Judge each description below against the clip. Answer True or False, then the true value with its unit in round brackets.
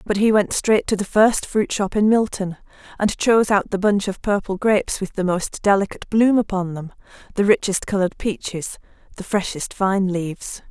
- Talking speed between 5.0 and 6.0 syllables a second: True (5.2 syllables/s)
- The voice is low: False (200 Hz)